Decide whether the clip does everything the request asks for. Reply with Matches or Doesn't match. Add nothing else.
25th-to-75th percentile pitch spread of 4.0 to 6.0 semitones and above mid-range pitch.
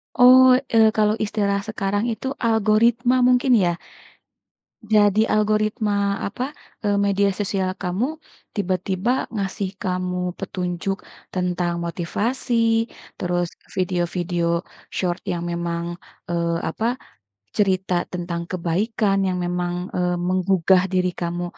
Doesn't match